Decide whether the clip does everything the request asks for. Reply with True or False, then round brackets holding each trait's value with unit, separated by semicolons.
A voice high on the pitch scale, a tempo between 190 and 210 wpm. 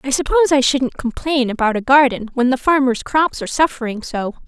True (260 Hz; 200 wpm)